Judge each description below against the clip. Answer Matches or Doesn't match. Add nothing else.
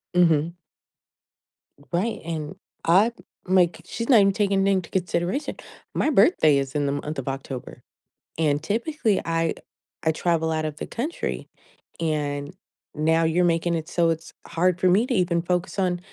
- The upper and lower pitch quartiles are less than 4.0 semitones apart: Matches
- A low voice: Doesn't match